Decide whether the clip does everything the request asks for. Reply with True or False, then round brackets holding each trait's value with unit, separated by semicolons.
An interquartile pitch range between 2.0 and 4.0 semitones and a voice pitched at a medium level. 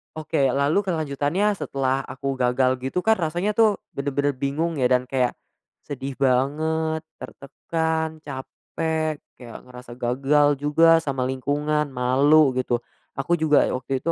True (3.3 semitones; 145 Hz)